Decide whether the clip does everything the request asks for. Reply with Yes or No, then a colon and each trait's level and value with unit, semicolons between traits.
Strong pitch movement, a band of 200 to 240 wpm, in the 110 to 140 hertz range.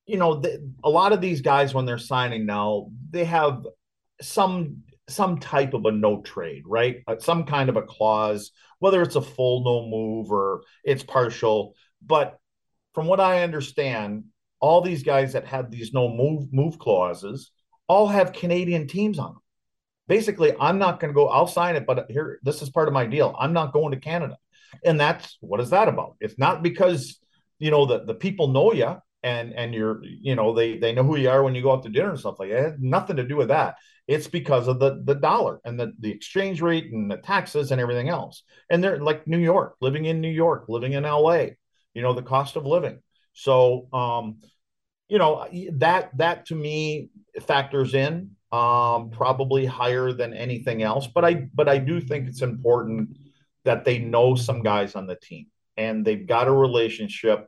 Yes: wide, 5.8 semitones; fast, 205 wpm; low, 135 Hz